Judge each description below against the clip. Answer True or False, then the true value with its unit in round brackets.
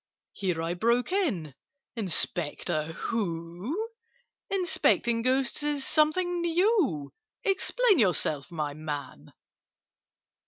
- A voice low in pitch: False (235 Hz)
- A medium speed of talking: False (80 wpm)